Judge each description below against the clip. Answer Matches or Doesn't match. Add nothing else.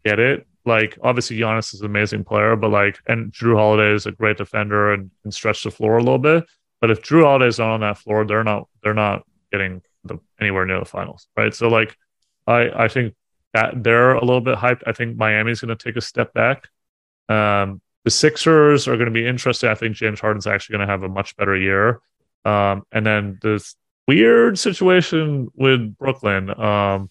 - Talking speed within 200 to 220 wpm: Matches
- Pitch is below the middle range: Matches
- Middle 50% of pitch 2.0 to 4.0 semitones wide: Matches